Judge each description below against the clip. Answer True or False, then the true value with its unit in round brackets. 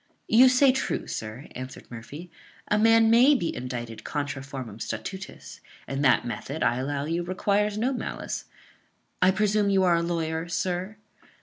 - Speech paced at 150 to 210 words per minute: True (160 wpm)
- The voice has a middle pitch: True (170 Hz)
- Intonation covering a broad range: True (7.6 semitones)